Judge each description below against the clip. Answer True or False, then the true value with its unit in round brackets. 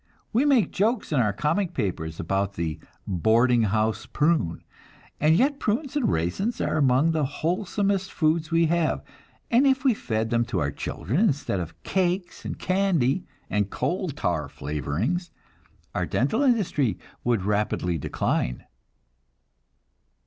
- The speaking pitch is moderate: True (145 Hz)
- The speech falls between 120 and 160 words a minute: True (140 wpm)